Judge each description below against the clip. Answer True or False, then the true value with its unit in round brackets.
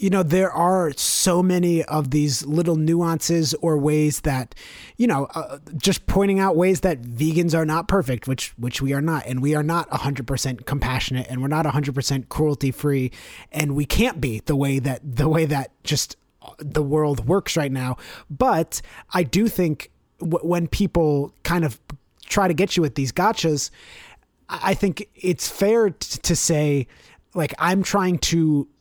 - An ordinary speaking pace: True (185 wpm)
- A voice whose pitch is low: False (155 Hz)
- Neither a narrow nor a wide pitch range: True (4.0 semitones)